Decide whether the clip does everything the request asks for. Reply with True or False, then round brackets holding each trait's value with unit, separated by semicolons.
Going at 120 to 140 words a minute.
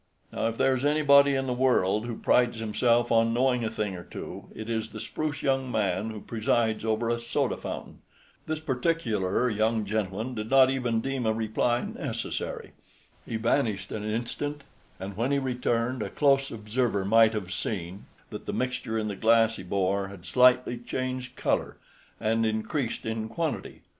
False (175 wpm)